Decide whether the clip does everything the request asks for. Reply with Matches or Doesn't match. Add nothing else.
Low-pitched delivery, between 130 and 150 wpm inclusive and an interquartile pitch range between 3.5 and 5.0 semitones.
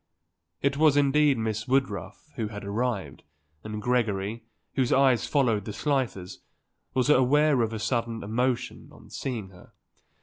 Matches